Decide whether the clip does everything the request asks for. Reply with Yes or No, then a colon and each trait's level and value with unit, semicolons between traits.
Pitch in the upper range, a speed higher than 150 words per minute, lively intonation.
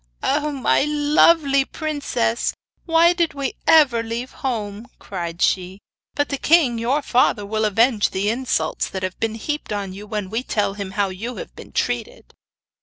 Yes: high, 230 Hz; average, 170 wpm; wide, 6.1 semitones